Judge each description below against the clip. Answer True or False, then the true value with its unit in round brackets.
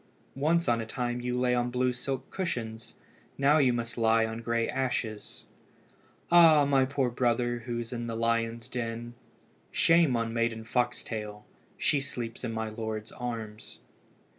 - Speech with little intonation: True (2.0 semitones)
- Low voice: True (120 Hz)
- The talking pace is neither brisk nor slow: True (155 wpm)